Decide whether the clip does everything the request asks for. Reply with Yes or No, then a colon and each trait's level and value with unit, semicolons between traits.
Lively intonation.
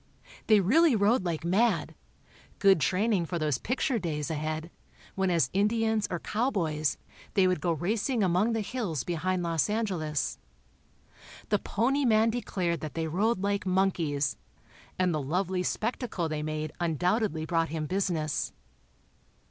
No: average, 5.0 semitones